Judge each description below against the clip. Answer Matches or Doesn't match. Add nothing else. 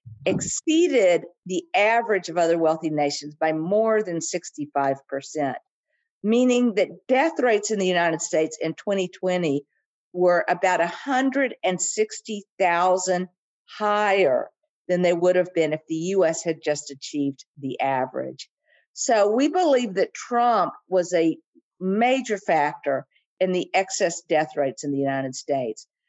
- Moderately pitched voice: Matches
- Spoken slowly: Matches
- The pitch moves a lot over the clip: Matches